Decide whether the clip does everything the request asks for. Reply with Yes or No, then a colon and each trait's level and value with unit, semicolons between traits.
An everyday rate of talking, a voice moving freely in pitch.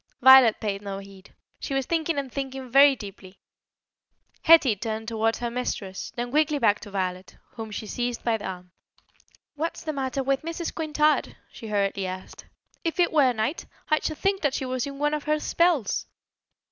Yes: average, 185 wpm; wide, 6.0 semitones